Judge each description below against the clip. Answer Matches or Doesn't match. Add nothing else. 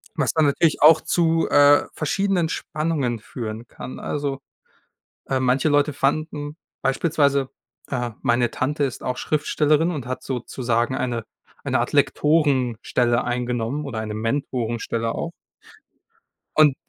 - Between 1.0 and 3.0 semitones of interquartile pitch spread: Doesn't match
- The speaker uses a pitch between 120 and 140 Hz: Matches